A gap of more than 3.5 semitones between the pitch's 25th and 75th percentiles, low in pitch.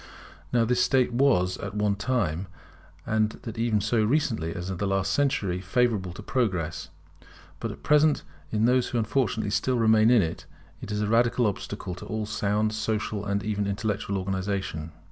No: average, 3.1 semitones; low, 105 Hz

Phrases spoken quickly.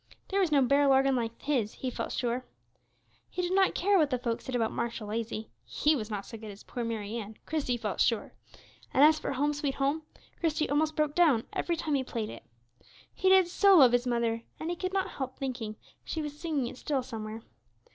Yes: fast, 220 wpm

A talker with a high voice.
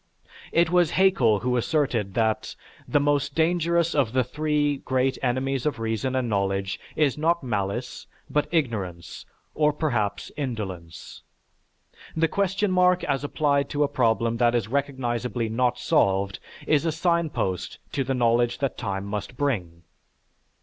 No: low, 130 Hz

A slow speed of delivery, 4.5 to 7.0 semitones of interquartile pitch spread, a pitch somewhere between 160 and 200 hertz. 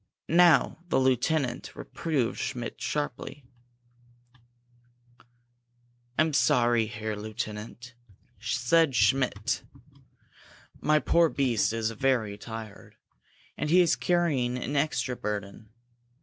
No: slow, 90 wpm; average, 5.1 semitones; low, 125 Hz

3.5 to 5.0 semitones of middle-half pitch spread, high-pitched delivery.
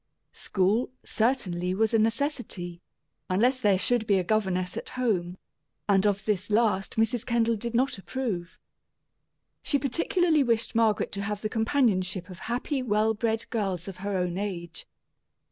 Yes: average, 4.0 semitones; high, 215 Hz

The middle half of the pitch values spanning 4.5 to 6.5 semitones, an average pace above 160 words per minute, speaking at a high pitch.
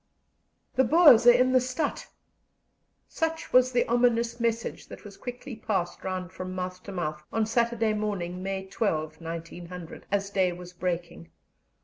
No: average, 5.0 semitones; average, 150 wpm; high, 200 Hz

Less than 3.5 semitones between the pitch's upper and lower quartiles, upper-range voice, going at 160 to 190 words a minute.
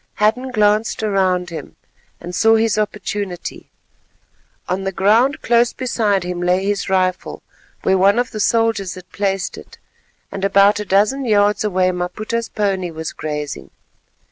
No: average, 2.9 semitones; high, 200 Hz; average, 145 wpm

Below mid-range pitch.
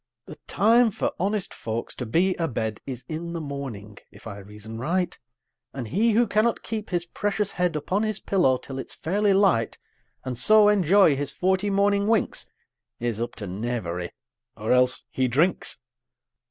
No: medium, 165 Hz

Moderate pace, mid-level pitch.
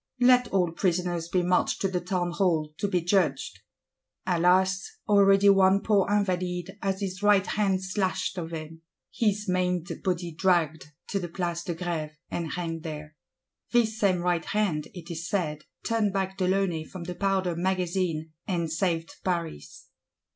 Yes: average, 155 wpm; medium, 180 Hz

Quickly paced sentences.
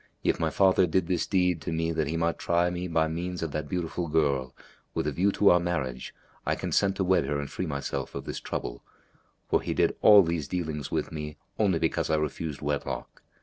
Yes: fast, 220 wpm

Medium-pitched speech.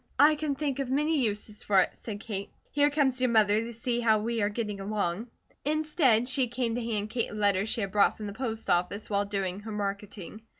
No: high, 220 Hz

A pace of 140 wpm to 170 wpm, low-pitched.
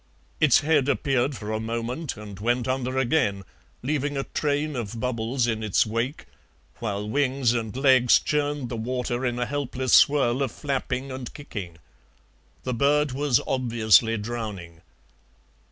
Yes: average, 145 wpm; low, 125 Hz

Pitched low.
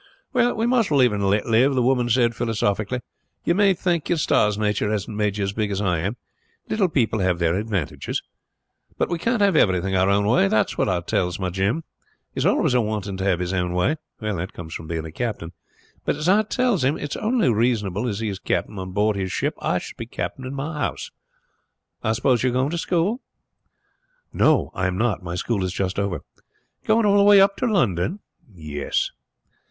Yes: low, 110 Hz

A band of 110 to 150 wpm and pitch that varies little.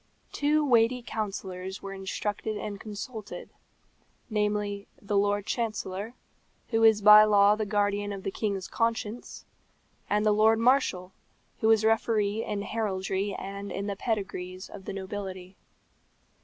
Yes: slow, 135 wpm; narrow, 1.9 semitones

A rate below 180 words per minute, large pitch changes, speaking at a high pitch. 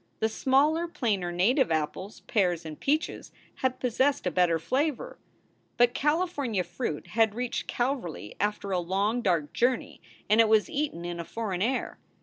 Yes: average, 155 wpm; wide, 6.7 semitones; high, 220 Hz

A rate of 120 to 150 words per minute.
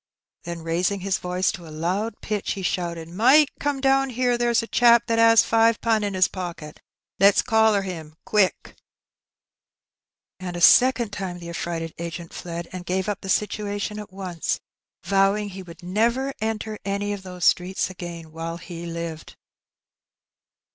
No: average, 175 wpm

